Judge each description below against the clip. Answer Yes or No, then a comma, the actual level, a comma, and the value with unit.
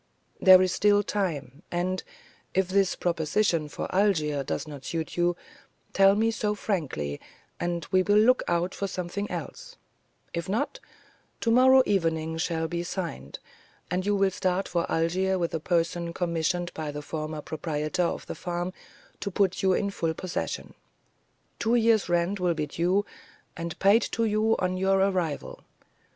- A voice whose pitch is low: No, medium, 180 Hz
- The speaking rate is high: No, average, 160 wpm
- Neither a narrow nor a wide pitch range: Yes, average, 3.4 semitones